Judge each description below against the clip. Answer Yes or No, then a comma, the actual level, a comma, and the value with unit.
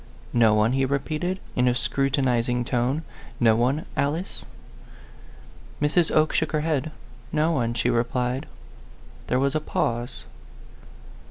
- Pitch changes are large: No, average, 4.0 semitones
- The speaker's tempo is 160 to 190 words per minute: No, average, 145 wpm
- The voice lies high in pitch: No, low, 135 Hz